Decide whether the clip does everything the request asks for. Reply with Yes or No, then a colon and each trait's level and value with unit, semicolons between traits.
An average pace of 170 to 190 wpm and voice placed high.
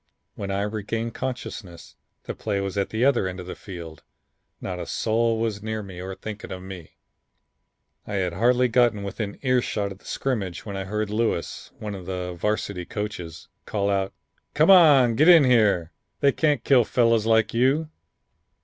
No: average, 180 wpm; low, 105 Hz